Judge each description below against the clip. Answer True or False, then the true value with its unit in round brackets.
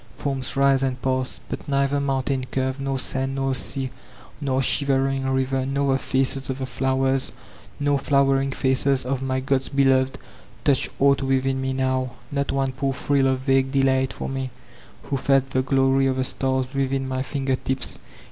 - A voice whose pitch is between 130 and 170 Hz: True (135 Hz)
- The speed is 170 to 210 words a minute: True (175 wpm)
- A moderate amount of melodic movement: False (0.7 semitones)